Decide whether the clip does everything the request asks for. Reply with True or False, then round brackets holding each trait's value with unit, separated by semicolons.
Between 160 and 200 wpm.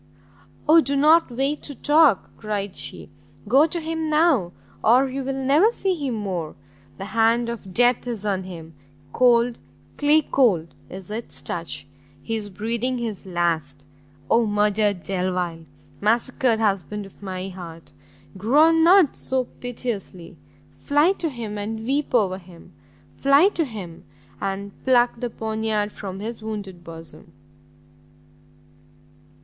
False (135 wpm)